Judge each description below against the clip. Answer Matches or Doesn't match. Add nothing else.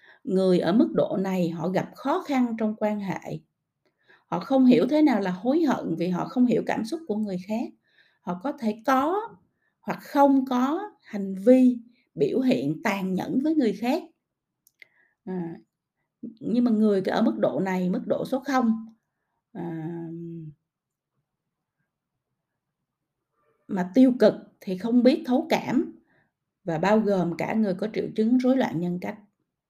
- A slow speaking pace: Matches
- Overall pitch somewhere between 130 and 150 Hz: Doesn't match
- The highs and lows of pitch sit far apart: Matches